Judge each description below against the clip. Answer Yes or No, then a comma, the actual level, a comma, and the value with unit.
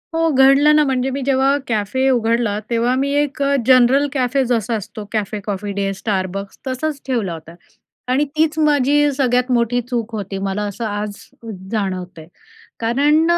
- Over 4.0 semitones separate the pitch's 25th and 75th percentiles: Yes, average, 4.7 semitones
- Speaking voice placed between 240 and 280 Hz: Yes, high, 245 Hz